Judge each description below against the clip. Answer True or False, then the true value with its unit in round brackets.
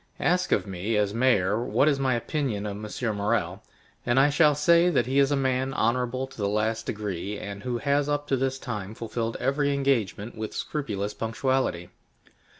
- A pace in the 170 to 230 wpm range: True (185 wpm)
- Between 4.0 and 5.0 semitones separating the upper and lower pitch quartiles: True (4.5 semitones)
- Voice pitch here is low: True (120 Hz)